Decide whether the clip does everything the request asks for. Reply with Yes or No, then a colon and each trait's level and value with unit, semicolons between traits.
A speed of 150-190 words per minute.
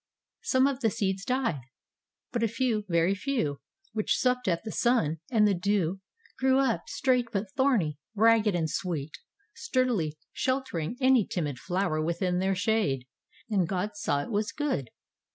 Yes: average, 155 wpm